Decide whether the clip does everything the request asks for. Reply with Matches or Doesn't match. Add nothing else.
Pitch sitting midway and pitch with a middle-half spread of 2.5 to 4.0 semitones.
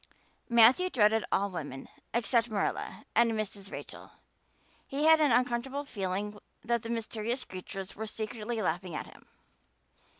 Doesn't match